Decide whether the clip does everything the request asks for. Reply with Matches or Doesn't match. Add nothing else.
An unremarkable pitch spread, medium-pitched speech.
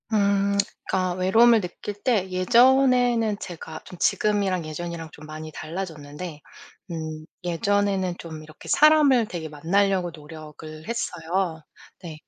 Matches